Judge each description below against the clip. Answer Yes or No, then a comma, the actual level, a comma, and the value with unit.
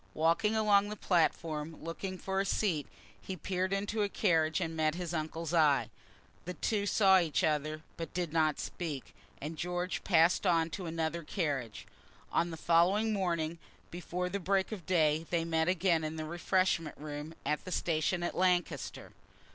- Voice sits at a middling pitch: Yes, medium, 170 Hz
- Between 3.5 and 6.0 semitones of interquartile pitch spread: No, average, 2.9 semitones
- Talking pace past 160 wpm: Yes, average, 170 wpm